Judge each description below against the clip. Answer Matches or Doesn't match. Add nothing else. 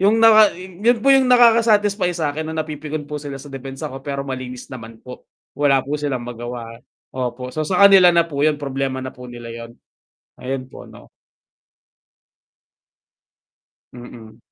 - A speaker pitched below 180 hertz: Matches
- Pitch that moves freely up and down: Matches